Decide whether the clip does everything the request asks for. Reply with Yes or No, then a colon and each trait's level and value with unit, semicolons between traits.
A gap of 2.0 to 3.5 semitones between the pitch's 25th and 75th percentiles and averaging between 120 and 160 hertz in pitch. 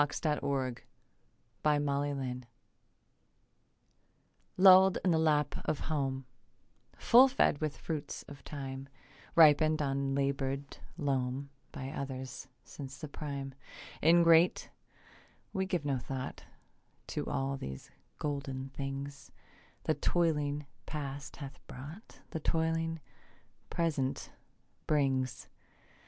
Yes: narrow, 2.4 semitones; medium, 140 Hz